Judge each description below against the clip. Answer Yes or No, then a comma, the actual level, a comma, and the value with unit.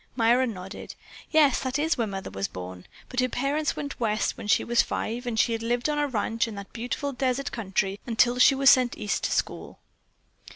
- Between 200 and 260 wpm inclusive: Yes, fast, 205 wpm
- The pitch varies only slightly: No, average, 3.9 semitones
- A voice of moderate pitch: No, high, 240 Hz